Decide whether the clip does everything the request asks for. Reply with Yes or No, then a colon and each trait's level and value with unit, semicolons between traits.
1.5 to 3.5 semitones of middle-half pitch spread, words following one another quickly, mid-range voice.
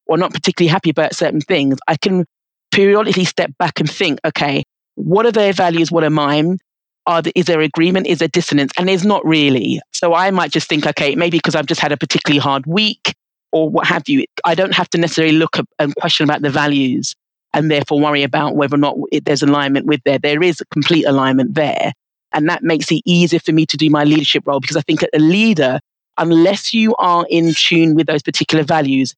Yes: average, 2.9 semitones; fast, 225 wpm; medium, 160 Hz